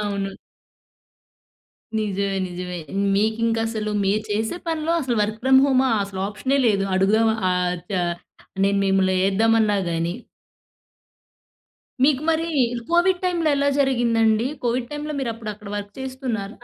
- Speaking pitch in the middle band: No, high, 220 Hz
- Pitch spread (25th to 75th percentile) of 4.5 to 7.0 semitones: Yes, average, 4.8 semitones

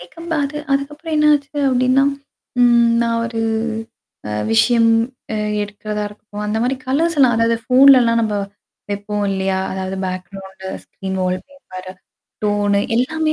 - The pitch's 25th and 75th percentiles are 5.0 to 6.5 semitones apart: Yes, wide, 5.4 semitones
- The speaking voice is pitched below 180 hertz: No, high, 230 Hz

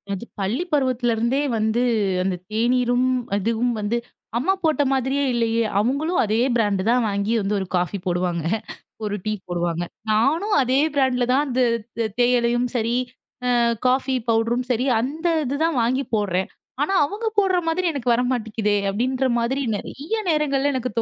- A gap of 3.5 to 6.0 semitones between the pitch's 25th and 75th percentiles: Yes, average, 3.8 semitones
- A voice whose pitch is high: Yes, high, 240 Hz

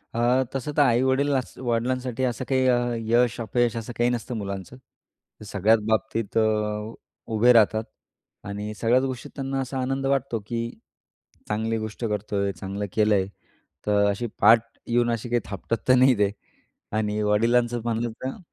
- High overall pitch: No, low, 115 Hz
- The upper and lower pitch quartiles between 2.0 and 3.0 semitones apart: Yes, average, 2.7 semitones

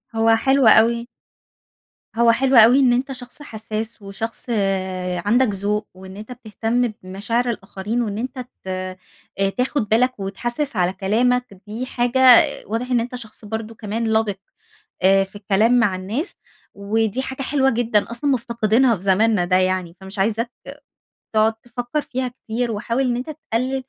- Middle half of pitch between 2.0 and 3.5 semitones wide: Yes, average, 3.2 semitones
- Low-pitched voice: No, high, 230 Hz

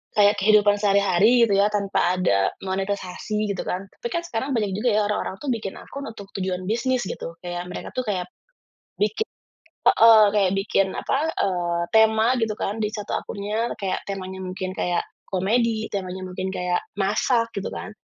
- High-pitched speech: Yes, high, 200 Hz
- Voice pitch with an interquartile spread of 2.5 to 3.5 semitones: Yes, average, 2.9 semitones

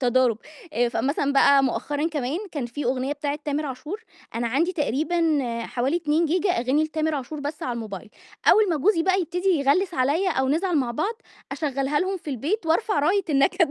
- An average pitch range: Yes, average, 4.3 semitones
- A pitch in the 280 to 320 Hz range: Yes, very high, 295 Hz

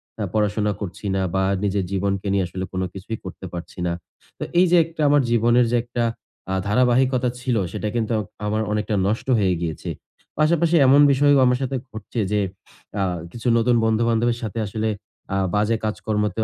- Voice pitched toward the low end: Yes, low, 110 Hz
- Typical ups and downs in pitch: Yes, average, 3.3 semitones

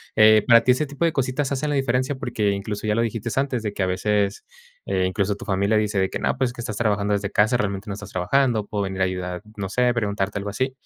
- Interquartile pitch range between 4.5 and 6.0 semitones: No, average, 3.8 semitones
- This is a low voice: Yes, low, 105 Hz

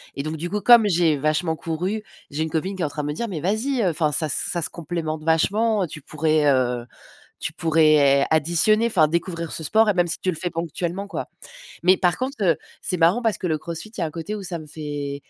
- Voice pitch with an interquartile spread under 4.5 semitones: Yes, average, 3.7 semitones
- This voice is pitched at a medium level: Yes, medium, 165 Hz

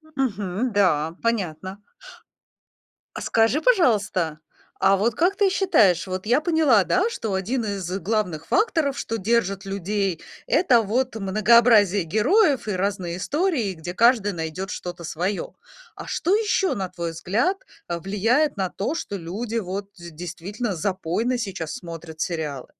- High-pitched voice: Yes, high, 200 Hz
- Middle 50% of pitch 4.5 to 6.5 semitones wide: Yes, average, 5.0 semitones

